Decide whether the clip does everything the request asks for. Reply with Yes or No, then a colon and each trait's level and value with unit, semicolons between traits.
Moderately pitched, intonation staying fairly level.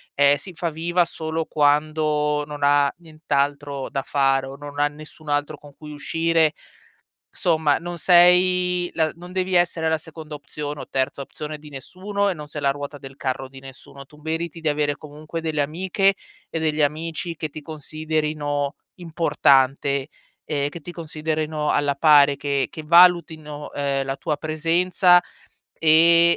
Yes: medium, 155 Hz; narrow, 2.3 semitones